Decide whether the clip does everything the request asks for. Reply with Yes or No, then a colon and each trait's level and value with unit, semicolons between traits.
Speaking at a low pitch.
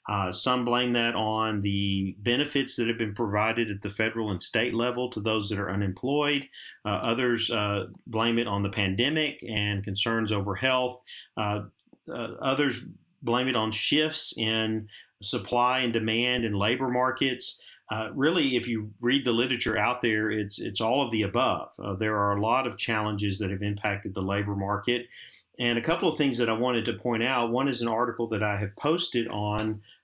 Yes: low, 115 Hz